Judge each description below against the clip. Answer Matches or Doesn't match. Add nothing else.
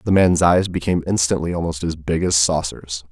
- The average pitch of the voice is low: Matches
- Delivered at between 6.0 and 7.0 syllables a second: Doesn't match